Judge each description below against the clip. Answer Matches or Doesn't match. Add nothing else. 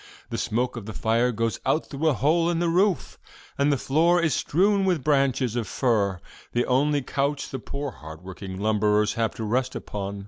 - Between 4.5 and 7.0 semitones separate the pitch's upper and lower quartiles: Matches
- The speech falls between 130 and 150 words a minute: Doesn't match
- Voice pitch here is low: Matches